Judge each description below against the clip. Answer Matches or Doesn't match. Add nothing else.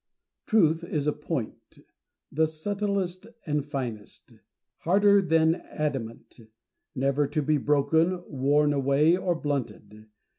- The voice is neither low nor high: Matches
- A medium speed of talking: Doesn't match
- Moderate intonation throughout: Matches